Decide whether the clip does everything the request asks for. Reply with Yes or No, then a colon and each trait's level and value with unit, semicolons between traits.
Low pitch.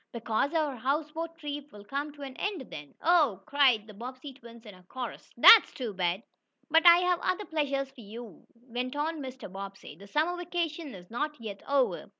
No: very high, 270 Hz